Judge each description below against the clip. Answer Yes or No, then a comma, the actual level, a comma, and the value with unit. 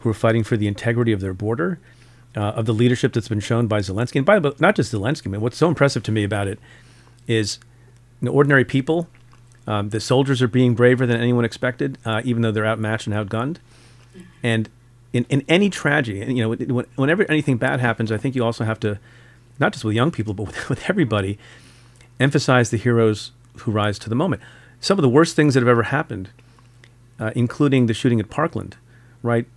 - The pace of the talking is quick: Yes, fast, 215 wpm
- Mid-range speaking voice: No, low, 120 Hz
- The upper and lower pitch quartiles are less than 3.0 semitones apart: Yes, narrow, 2.4 semitones